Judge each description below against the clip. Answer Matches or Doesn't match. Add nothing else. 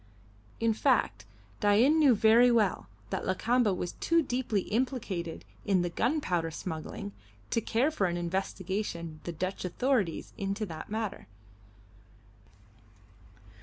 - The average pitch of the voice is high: Matches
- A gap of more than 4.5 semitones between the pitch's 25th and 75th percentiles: Matches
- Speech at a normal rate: Doesn't match